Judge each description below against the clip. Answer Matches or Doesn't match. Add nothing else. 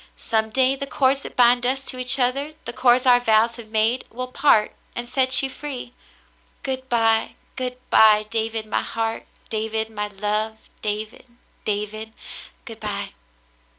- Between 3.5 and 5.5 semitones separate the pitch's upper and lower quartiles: Doesn't match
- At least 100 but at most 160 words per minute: Matches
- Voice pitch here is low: Doesn't match